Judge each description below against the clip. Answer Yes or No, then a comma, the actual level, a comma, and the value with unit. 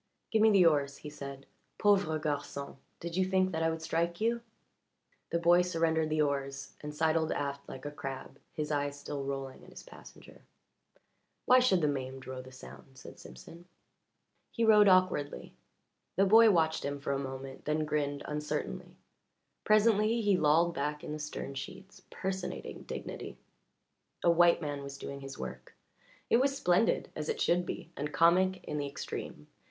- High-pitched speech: No, medium, 155 Hz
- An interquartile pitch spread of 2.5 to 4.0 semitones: No, average, 4.6 semitones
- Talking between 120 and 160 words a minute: No, average, 170 wpm